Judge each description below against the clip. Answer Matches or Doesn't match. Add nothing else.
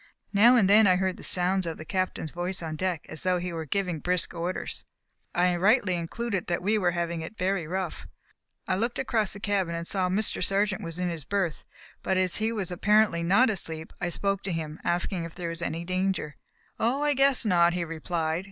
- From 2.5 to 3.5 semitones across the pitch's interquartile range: Matches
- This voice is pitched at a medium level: Matches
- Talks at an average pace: Doesn't match